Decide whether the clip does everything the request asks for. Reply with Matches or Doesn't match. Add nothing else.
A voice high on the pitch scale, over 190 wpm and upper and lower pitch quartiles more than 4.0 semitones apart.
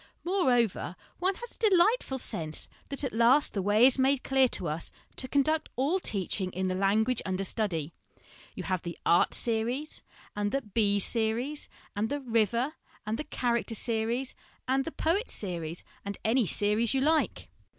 Matches